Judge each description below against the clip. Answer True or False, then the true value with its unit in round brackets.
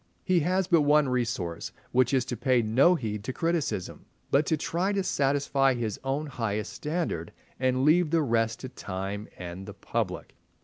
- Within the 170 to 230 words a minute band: True (175 wpm)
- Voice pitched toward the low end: True (130 Hz)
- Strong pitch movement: True (5.8 semitones)